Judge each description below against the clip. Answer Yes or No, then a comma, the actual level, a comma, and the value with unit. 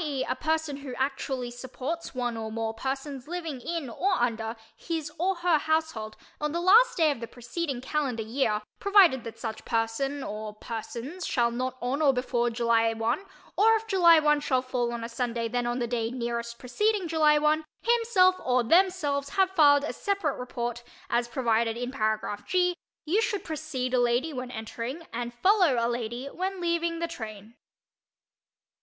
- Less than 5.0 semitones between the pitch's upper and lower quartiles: No, wide, 5.6 semitones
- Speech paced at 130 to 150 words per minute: No, average, 175 wpm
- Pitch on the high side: Yes, very high, 260 Hz